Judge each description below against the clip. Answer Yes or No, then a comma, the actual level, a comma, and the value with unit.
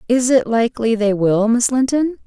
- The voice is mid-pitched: No, high, 235 Hz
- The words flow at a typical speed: Yes, average, 185 wpm